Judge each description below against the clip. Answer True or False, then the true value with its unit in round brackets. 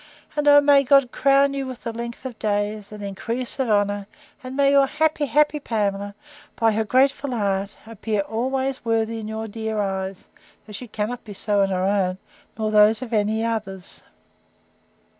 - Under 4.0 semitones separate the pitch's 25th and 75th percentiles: False (4.3 semitones)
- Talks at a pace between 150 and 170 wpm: False (180 wpm)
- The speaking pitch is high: True (225 Hz)